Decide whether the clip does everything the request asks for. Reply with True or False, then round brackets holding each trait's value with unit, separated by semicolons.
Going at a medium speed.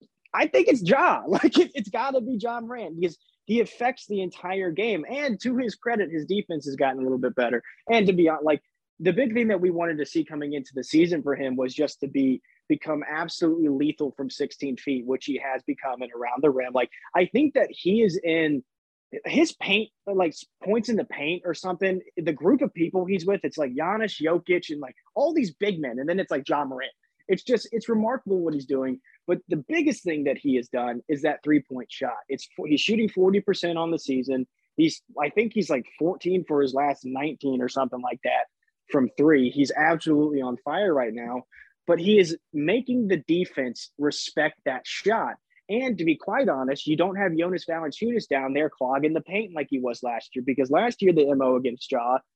False (220 wpm)